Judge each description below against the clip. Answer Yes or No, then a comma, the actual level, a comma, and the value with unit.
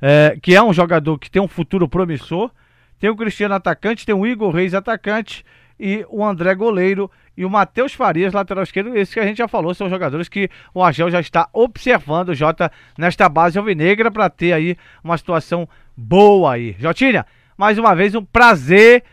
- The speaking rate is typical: No, fast, 190 wpm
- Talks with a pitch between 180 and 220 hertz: Yes, high, 190 Hz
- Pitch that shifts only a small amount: No, average, 3.6 semitones